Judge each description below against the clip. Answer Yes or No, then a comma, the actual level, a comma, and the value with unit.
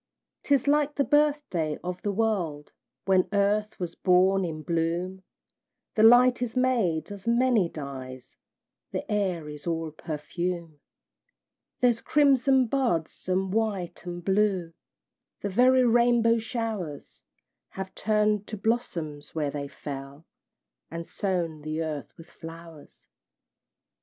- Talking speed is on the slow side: Yes, slow, 120 wpm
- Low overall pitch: No, high, 190 Hz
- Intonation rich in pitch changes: Yes, wide, 5.8 semitones